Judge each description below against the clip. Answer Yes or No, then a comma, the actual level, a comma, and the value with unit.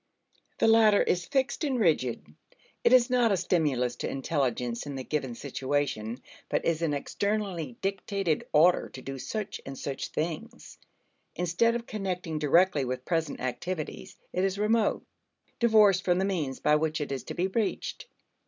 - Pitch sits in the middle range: Yes, medium, 170 Hz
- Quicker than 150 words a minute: Yes, average, 160 wpm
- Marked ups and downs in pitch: Yes, wide, 6.2 semitones